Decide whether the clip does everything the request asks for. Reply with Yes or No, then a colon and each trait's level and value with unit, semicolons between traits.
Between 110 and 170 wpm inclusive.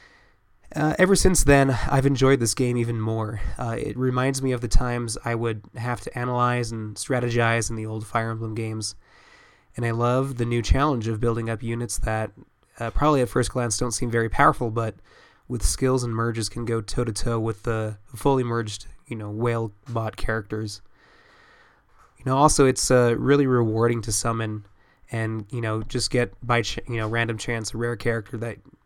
No: average, 195 wpm